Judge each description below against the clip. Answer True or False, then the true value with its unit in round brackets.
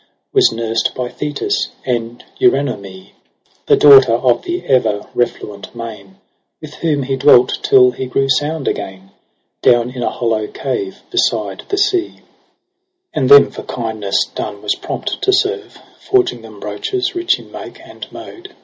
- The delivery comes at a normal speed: True (155 wpm)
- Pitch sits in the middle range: False (130 Hz)